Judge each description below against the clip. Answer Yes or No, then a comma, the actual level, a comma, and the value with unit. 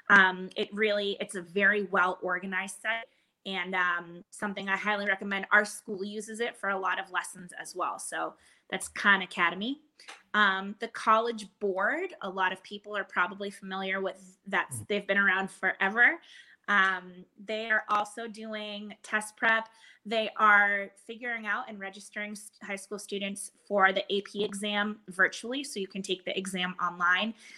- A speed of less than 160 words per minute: No, average, 165 wpm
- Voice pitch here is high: Yes, high, 200 Hz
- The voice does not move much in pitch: Yes, narrow, 2.0 semitones